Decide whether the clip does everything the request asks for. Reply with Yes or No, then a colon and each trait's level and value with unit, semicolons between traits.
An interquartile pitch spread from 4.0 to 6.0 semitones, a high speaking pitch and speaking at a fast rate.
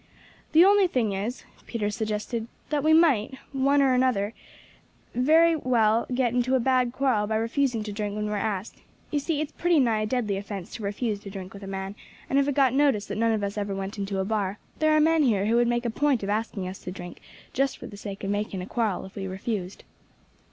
Yes: average, 4.7 semitones; high, 225 Hz; fast, 235 wpm